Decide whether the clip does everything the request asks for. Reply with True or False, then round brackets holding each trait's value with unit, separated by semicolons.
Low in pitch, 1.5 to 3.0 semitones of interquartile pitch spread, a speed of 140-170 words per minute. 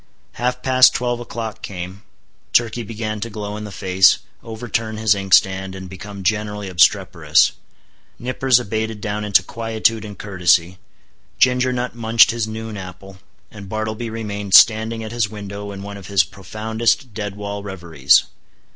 True (105 Hz; 2.5 semitones; 150 wpm)